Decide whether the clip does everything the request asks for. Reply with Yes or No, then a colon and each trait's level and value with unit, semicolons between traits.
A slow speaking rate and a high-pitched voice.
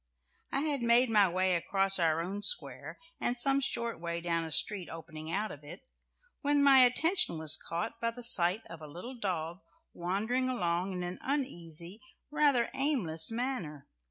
No: average, 170 wpm; high, 195 Hz